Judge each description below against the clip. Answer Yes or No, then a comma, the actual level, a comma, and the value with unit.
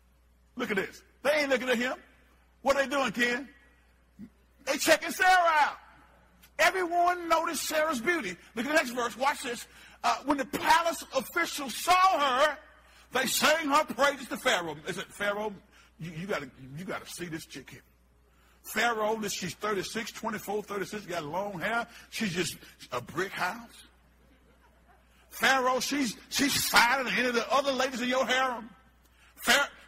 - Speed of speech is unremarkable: Yes, average, 160 wpm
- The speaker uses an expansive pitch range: Yes, wide, 7.2 semitones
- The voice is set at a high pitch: Yes, high, 245 Hz